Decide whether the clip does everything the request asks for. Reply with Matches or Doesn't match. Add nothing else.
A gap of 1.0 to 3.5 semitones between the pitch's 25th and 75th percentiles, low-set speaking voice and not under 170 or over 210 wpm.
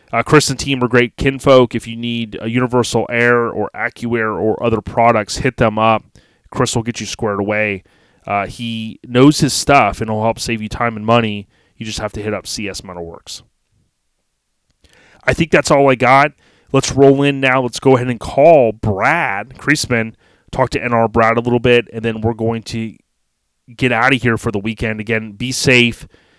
Matches